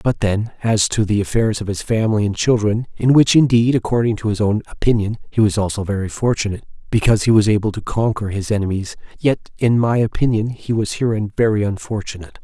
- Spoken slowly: No, average, 200 wpm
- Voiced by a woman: No, male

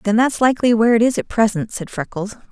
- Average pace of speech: No, fast, 240 wpm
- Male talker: No, female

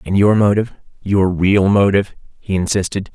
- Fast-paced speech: No, slow, 135 wpm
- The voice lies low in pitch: Yes, low, 100 Hz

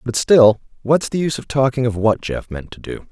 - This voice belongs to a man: Yes, male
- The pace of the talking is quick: Yes, fast, 230 wpm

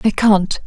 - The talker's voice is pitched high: Yes, high, 200 Hz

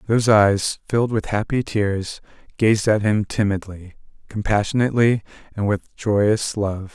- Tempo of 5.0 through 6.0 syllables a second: No, 4.4 syllables/s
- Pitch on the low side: Yes, low, 105 Hz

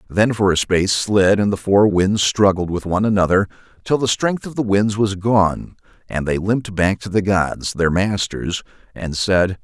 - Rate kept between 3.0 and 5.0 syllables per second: Yes, 4.6 syllables/s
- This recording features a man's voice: Yes, male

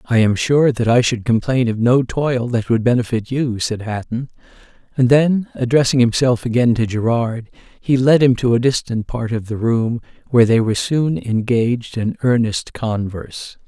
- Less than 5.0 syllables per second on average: Yes, 4.8 syllables/s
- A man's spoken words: Yes, male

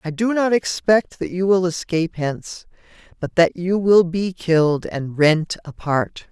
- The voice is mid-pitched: Yes, medium, 175 Hz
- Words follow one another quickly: No, average, 170 wpm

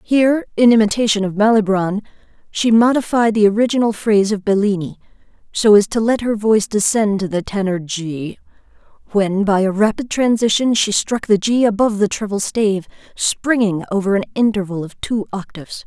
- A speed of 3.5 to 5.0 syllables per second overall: No, 5.5 syllables/s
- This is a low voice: No, high, 210 Hz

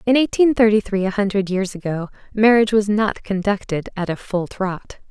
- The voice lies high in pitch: Yes, high, 200 Hz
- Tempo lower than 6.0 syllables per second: Yes, 5.2 syllables/s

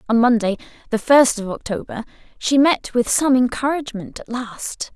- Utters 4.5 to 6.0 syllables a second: Yes, 4.9 syllables/s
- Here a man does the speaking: No, female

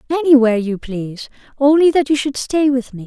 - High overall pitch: Yes, very high, 265 Hz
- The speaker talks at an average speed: Yes, average, 195 wpm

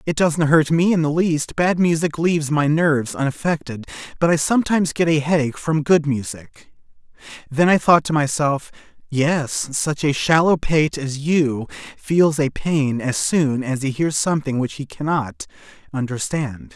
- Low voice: No, medium, 150 Hz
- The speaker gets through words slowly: No, average, 170 wpm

